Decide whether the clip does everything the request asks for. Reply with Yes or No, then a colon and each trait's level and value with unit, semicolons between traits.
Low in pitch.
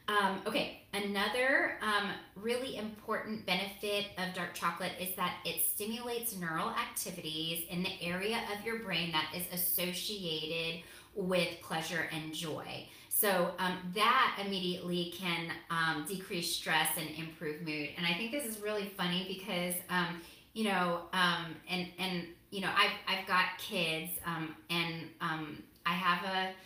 No: medium, 180 Hz